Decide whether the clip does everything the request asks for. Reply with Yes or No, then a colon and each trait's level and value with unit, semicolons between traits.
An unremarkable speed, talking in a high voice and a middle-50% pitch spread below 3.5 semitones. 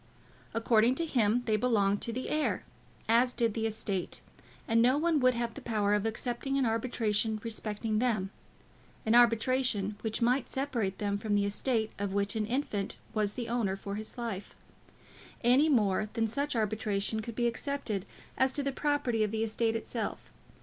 Yes: average, 175 wpm; high, 225 Hz; average, 2.9 semitones